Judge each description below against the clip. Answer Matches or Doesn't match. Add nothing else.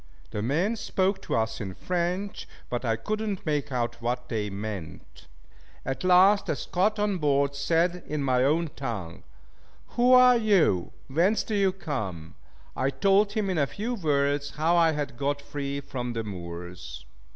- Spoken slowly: Doesn't match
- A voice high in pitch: Doesn't match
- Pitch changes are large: Matches